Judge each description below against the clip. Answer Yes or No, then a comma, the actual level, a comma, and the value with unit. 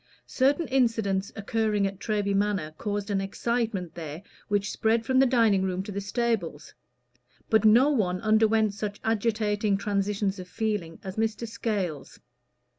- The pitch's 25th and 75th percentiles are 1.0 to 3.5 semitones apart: Yes, narrow, 2.4 semitones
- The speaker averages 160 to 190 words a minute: No, average, 145 wpm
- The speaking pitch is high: Yes, high, 210 Hz